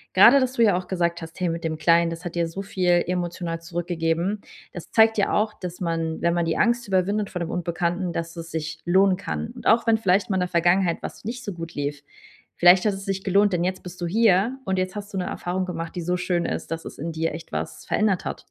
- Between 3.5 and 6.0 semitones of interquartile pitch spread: No, average, 2.7 semitones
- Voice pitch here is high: No, medium, 180 Hz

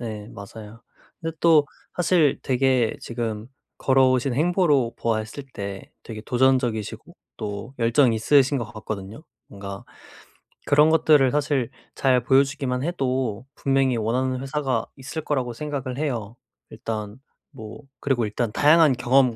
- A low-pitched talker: Yes, low, 130 Hz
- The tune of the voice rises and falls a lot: No, average, 3.9 semitones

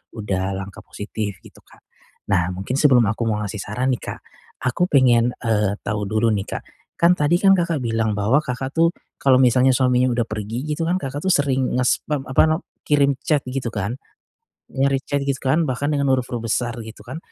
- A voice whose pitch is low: Yes, low, 125 Hz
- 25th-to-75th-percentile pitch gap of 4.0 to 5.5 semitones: Yes, average, 4.4 semitones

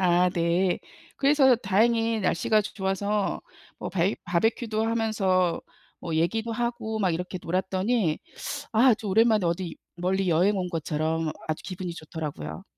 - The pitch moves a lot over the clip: No, average, 4.3 semitones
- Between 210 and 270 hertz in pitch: No, high, 190 Hz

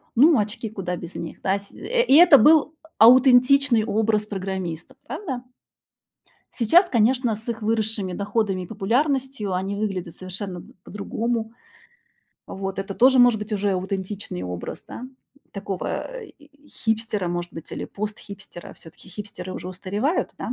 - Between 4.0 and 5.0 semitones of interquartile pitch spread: Yes, average, 4.4 semitones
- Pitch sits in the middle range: No, high, 210 Hz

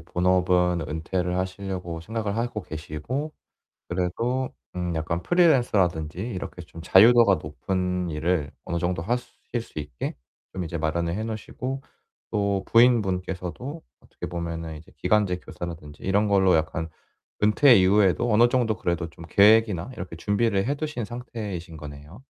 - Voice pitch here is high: No, very low, 95 Hz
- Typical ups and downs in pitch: Yes, average, 4.7 semitones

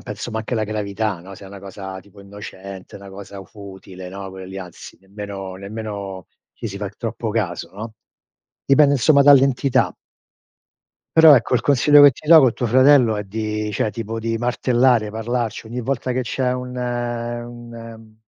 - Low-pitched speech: Yes, low, 110 Hz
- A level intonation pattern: No, average, 3.7 semitones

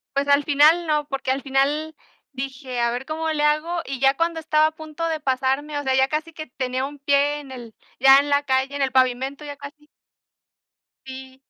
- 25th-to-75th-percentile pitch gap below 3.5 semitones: Yes, narrow, 2.4 semitones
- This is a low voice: No, very high, 280 Hz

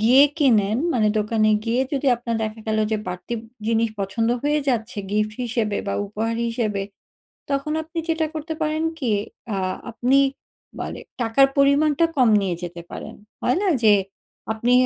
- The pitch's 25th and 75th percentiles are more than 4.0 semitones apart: Yes, average, 4.4 semitones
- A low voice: No, high, 230 Hz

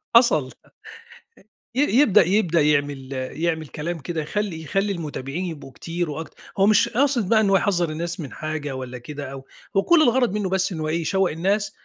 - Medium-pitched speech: Yes, medium, 170 Hz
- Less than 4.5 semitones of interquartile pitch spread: No, average, 4.8 semitones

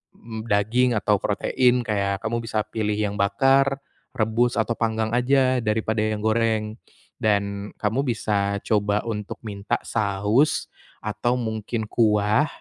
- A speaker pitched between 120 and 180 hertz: No, low, 110 Hz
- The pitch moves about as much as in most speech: No, narrow, 2.1 semitones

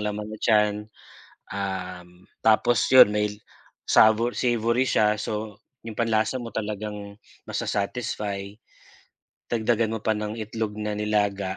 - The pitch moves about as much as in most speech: No, narrow, 1.4 semitones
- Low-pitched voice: Yes, low, 105 Hz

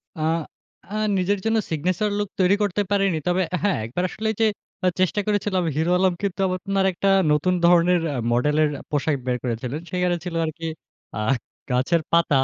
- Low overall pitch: No, medium, 180 Hz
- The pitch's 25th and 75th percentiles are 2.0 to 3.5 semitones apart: No, average, 3.9 semitones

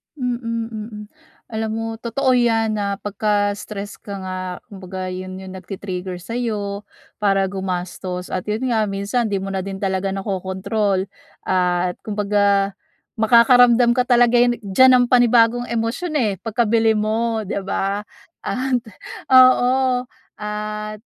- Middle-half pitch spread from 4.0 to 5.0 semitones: No, average, 3.2 semitones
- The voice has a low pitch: No, high, 210 Hz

